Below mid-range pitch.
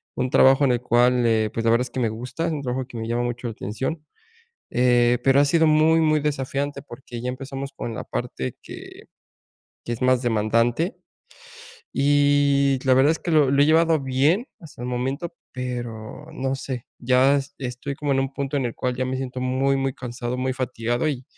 Yes: low, 130 Hz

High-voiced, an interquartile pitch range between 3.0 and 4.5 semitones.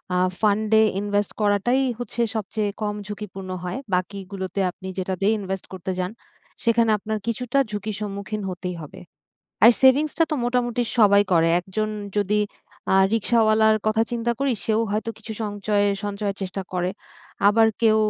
No: high, 210 Hz; narrow, 2.4 semitones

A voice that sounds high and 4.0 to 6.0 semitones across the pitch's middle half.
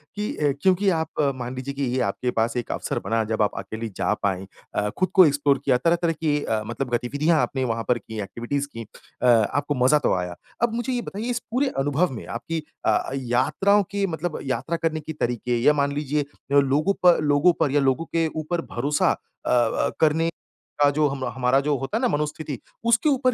No: medium, 145 Hz; average, 5.1 semitones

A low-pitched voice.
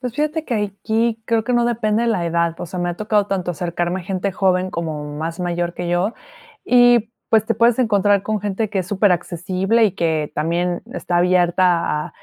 No: high, 190 Hz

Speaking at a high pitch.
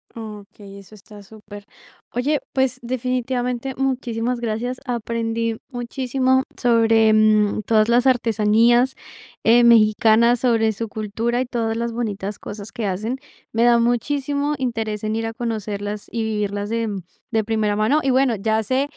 Yes: high, 230 Hz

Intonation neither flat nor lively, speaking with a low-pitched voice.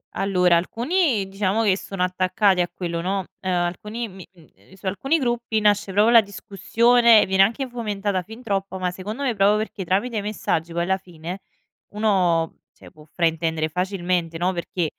No: average, 3.2 semitones; high, 195 Hz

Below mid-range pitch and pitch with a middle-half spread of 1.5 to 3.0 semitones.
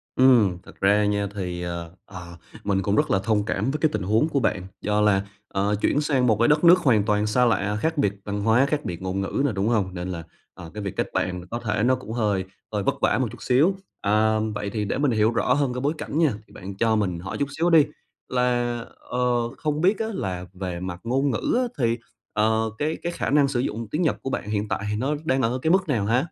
No: low, 110 Hz; average, 4.9 semitones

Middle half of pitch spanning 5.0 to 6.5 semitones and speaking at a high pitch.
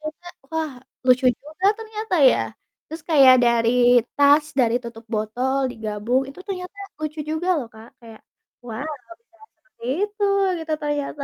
Yes: wide, 5.5 semitones; very high, 285 Hz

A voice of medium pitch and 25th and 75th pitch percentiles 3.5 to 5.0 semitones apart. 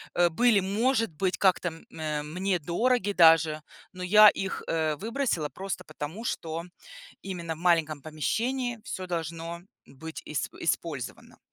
Yes: medium, 175 Hz; average, 4.0 semitones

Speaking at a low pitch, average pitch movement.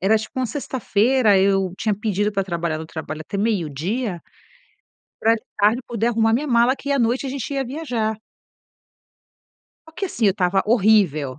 No: high, 215 Hz; average, 4.2 semitones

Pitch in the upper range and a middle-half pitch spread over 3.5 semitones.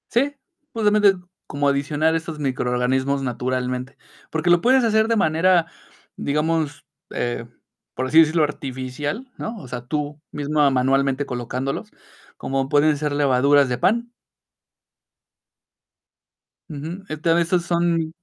No: medium, 150 Hz; average, 4.1 semitones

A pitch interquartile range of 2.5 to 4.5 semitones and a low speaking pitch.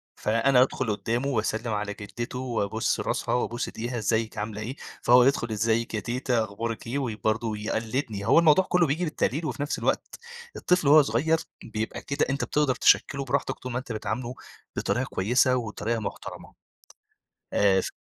Yes: average, 3.6 semitones; low, 120 Hz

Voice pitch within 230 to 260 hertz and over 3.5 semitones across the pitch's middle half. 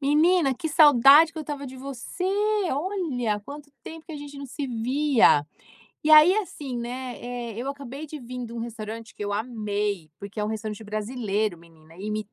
Yes: very high, 250 Hz; average, 5.2 semitones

